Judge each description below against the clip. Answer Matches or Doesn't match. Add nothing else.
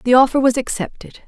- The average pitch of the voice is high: Matches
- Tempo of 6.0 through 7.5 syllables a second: Matches